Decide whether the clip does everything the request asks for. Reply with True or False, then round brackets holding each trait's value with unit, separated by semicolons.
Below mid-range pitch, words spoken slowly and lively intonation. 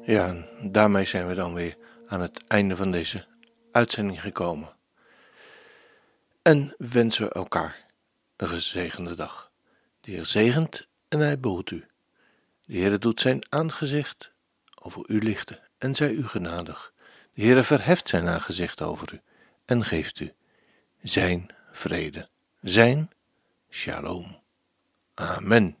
True (115 Hz; 130 wpm; 7.9 semitones)